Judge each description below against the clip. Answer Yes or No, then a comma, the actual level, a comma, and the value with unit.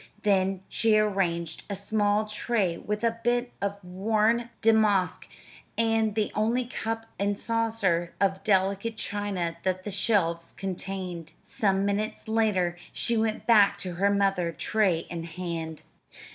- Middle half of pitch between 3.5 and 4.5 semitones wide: No, average, 3.1 semitones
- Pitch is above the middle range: Yes, high, 200 Hz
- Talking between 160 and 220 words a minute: No, slow, 135 wpm